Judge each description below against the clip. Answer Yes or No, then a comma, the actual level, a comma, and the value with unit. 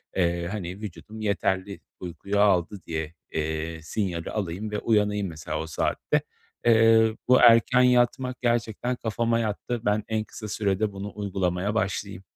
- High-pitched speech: No, low, 105 Hz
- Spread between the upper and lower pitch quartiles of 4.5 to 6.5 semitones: No, average, 3.6 semitones